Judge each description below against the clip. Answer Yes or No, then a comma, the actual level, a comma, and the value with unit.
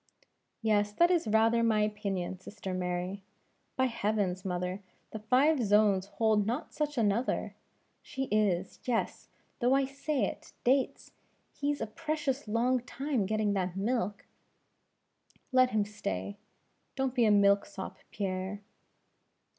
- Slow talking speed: Yes, slow, 130 wpm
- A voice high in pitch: Yes, high, 215 Hz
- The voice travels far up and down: No, average, 4.2 semitones